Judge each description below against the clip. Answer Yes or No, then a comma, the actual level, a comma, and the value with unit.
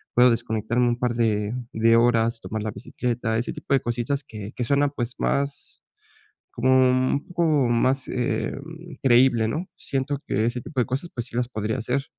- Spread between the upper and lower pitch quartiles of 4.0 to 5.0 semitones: No, average, 2.8 semitones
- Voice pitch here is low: Yes, low, 125 Hz